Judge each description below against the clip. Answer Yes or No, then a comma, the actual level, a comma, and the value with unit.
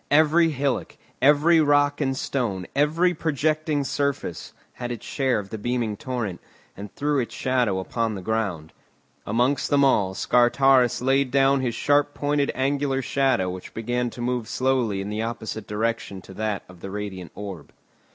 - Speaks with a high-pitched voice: No, low, 125 Hz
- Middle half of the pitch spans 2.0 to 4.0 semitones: No, average, 4.9 semitones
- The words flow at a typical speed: Yes, average, 160 wpm